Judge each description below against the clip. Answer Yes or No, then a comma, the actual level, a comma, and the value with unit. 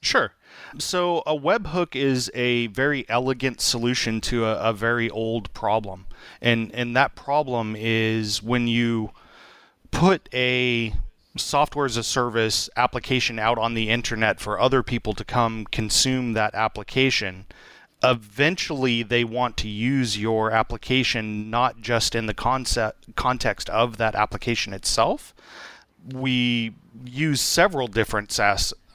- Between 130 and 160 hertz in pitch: No, low, 120 Hz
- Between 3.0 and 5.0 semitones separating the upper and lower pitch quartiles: No, narrow, 2.6 semitones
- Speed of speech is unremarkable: No, slow, 130 wpm